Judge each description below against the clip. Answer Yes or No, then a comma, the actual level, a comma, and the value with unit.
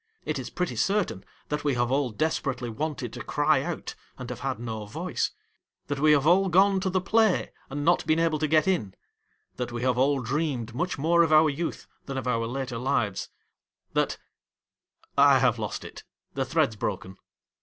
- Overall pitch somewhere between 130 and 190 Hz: Yes, medium, 140 Hz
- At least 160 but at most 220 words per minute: Yes, average, 190 wpm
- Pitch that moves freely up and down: No, average, 4.8 semitones